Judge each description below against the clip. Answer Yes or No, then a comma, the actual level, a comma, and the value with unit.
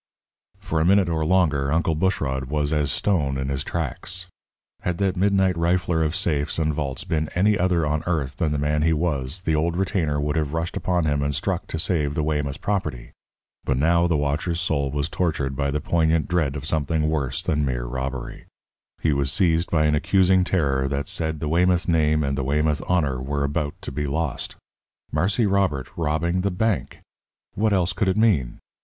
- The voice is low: Yes, very low, 80 Hz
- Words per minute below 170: No, average, 195 wpm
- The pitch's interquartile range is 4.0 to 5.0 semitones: No, average, 3.6 semitones